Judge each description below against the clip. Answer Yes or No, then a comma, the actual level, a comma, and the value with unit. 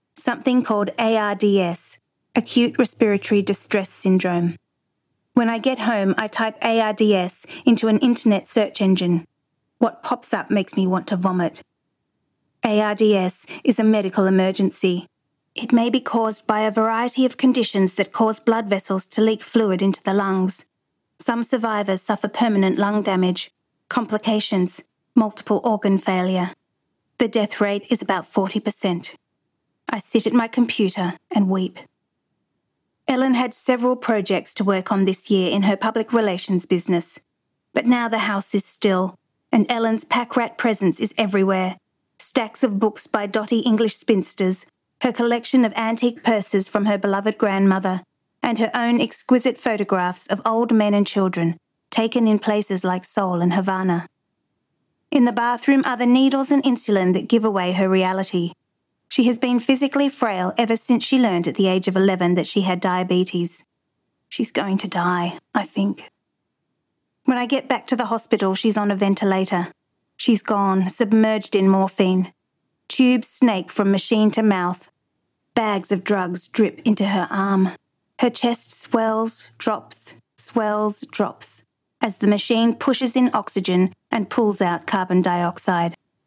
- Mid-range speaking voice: No, high, 210 Hz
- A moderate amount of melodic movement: Yes, average, 3.5 semitones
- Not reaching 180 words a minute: Yes, average, 150 wpm